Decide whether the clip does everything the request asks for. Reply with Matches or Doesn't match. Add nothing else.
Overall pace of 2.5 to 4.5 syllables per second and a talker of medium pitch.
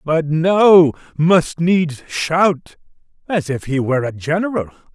Matches